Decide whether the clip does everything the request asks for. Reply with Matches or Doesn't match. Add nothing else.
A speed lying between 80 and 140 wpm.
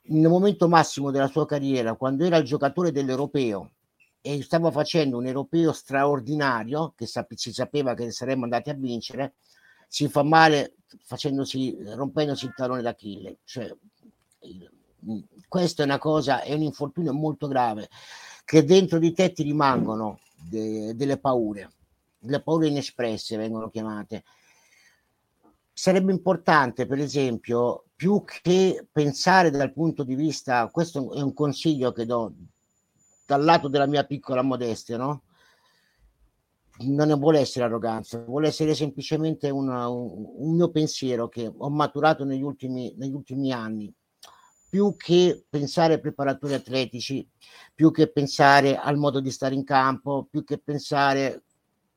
Matches